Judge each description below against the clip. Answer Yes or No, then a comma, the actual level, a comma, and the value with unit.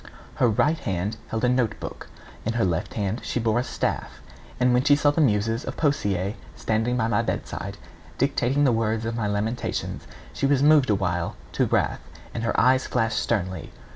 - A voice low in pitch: Yes, low, 115 Hz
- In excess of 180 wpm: Yes, average, 190 wpm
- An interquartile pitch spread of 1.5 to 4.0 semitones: Yes, average, 3.6 semitones